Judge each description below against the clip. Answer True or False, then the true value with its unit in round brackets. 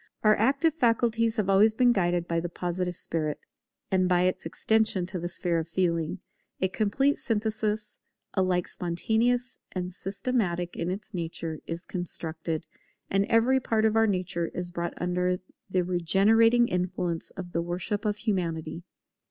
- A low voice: False (185 Hz)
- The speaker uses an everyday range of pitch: True (4.1 semitones)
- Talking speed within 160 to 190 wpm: False (150 wpm)